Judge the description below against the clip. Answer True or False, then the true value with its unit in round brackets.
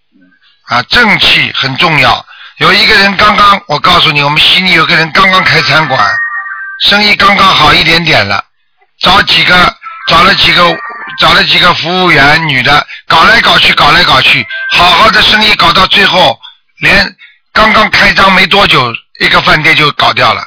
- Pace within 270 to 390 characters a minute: False (250 characters per minute)